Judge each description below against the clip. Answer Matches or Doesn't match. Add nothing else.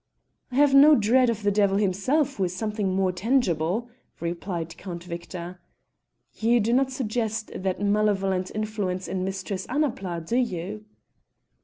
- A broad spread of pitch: Doesn't match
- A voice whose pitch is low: Doesn't match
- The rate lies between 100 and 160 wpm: Matches